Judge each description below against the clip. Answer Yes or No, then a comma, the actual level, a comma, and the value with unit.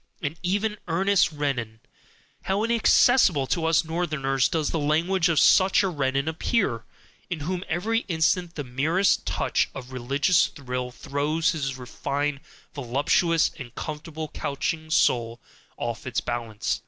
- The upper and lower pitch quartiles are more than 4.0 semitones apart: Yes, average, 4.6 semitones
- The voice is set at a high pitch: No, medium, 155 Hz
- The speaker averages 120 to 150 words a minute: Yes, slow, 135 wpm